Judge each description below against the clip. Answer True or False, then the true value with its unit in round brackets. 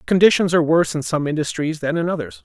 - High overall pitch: False (155 Hz)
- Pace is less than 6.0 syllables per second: False (6.9 syllables/s)